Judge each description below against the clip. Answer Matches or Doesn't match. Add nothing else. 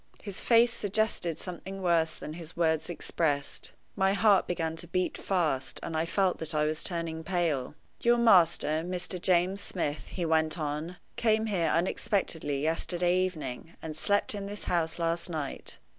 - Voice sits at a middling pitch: Matches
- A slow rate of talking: Doesn't match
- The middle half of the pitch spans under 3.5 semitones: Matches